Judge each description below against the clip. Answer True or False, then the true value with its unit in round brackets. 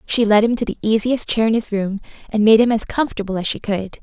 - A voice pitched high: True (215 Hz)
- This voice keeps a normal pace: False (270 wpm)